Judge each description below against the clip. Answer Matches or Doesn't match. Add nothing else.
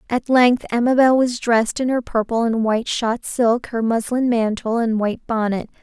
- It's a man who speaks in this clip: Doesn't match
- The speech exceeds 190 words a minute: Doesn't match